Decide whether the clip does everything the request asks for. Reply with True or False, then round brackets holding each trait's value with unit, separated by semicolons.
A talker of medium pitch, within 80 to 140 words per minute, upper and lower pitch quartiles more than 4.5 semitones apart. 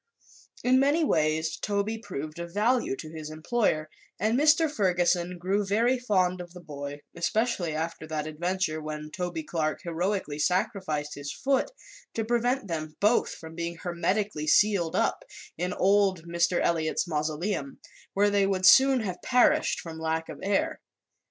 False (180 Hz; 150 wpm; 4.9 semitones)